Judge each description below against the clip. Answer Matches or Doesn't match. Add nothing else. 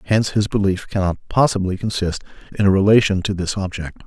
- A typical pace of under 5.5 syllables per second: Doesn't match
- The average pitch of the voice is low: Matches